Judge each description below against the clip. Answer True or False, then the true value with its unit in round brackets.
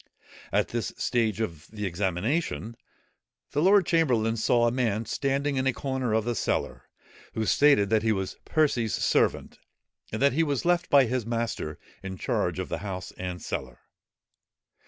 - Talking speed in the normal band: True (165 wpm)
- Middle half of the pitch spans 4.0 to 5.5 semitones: True (4.9 semitones)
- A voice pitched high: False (115 Hz)